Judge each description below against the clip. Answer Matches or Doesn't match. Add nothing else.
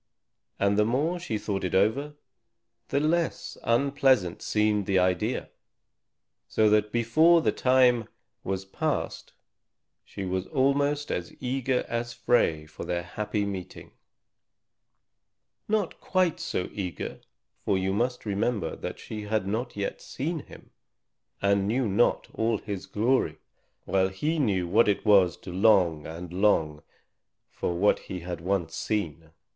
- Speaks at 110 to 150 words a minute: Matches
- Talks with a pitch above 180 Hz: Doesn't match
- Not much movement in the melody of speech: Doesn't match